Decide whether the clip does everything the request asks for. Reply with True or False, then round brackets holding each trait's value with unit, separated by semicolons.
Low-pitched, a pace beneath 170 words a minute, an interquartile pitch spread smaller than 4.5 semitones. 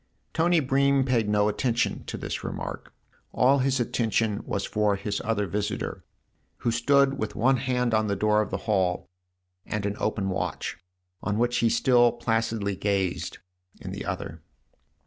True (115 Hz; 160 wpm; 3.3 semitones)